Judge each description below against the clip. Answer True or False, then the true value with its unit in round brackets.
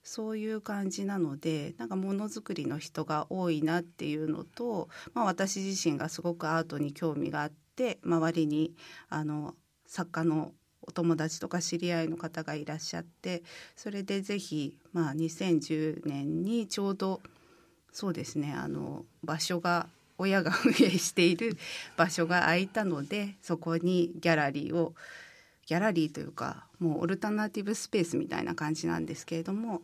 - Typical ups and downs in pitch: True (3.7 semitones)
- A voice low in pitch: False (170 Hz)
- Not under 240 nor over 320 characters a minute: True (310 characters per minute)